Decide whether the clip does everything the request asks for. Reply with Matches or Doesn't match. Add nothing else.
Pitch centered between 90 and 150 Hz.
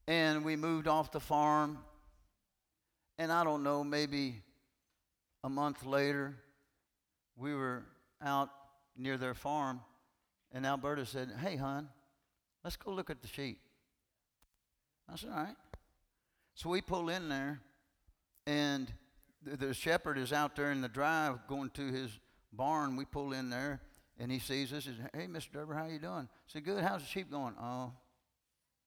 Matches